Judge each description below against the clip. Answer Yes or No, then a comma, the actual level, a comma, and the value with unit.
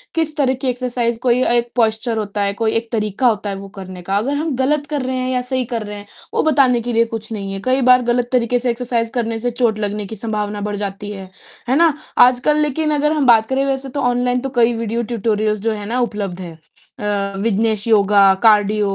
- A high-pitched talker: Yes, high, 230 Hz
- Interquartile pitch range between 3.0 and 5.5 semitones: Yes, average, 3.5 semitones